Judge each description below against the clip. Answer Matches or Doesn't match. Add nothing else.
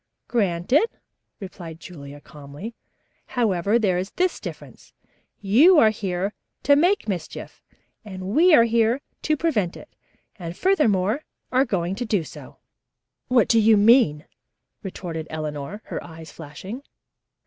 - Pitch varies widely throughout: Matches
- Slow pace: Matches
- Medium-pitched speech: Doesn't match